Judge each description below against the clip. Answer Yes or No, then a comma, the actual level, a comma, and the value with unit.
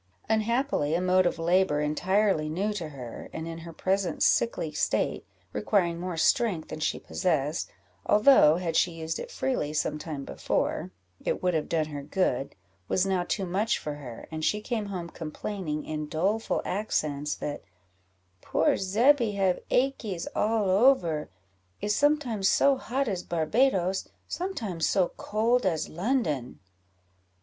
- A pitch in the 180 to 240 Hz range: Yes, medium, 185 Hz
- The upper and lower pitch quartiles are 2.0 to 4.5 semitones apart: No, average, 5.3 semitones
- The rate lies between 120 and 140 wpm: No, average, 150 wpm